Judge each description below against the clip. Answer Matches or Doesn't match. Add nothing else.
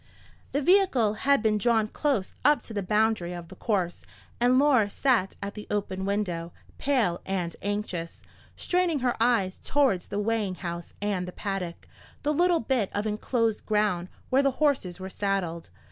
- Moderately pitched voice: Doesn't match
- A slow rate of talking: Doesn't match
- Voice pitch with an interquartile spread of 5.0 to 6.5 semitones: Matches